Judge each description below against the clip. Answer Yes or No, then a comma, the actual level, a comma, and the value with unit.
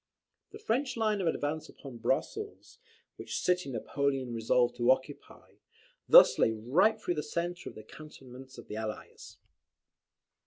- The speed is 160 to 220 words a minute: No, average, 145 wpm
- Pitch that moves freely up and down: Yes, wide, 6.7 semitones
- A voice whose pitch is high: No, medium, 140 Hz